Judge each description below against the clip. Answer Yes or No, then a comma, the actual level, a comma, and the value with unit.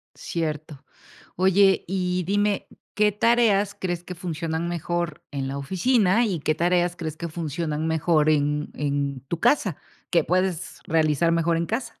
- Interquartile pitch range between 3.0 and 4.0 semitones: Yes, average, 3.4 semitones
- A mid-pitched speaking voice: Yes, medium, 170 Hz